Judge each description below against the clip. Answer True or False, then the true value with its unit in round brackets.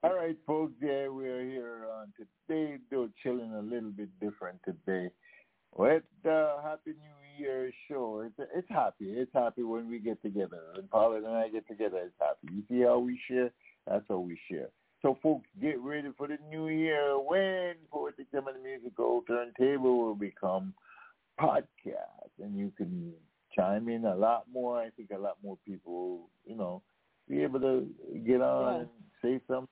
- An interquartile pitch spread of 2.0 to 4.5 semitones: False (4.9 semitones)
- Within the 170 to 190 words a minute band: True (185 wpm)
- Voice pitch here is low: True (125 Hz)